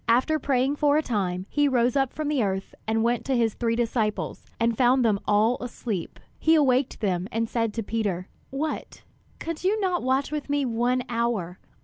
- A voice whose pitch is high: Yes, high, 240 Hz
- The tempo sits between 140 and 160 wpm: No, average, 195 wpm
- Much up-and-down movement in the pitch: No, average, 3.9 semitones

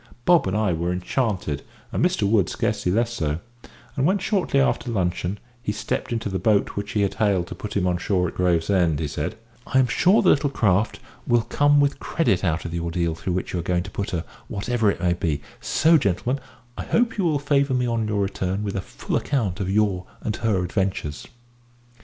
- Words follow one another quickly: Yes, fast, 220 wpm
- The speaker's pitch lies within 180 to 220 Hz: No, low, 100 Hz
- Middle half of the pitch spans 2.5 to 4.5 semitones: No, wide, 5.4 semitones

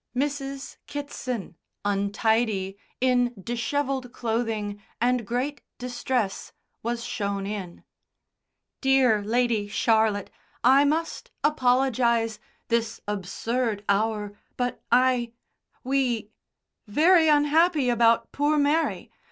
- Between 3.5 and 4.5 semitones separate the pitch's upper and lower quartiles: Yes, average, 3.8 semitones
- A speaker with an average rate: No, slow, 90 wpm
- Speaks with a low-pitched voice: No, high, 240 Hz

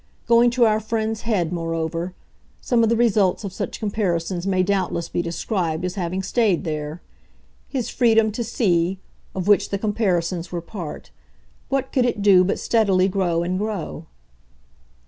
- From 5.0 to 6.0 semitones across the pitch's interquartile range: No, average, 4.2 semitones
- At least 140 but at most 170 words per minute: Yes, average, 160 wpm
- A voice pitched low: No, high, 190 Hz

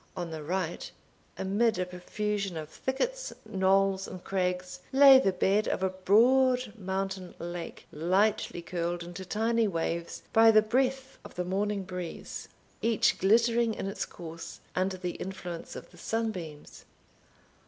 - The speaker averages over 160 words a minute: No, average, 145 wpm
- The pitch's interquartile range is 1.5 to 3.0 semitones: No, average, 3.8 semitones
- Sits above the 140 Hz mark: Yes, high, 190 Hz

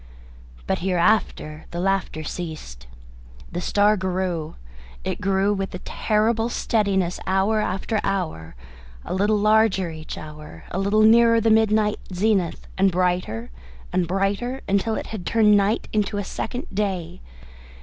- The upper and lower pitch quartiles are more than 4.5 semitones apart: No, average, 3.2 semitones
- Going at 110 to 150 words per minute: Yes, average, 140 wpm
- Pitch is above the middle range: Yes, high, 195 Hz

